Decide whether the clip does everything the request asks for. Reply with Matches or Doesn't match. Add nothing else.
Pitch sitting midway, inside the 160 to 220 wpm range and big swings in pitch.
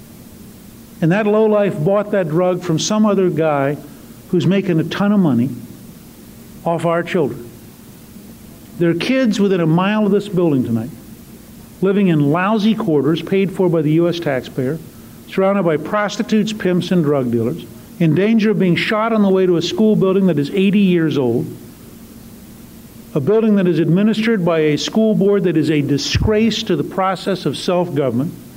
Doesn't match